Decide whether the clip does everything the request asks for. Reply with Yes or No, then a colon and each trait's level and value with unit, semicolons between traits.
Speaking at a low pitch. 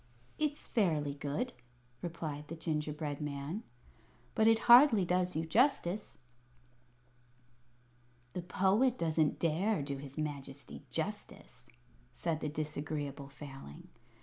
No: medium, 155 Hz